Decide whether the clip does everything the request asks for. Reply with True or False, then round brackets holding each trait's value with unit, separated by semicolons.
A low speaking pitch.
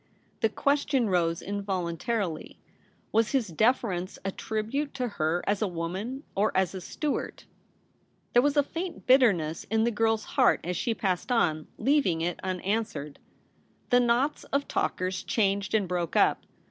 False (210 Hz)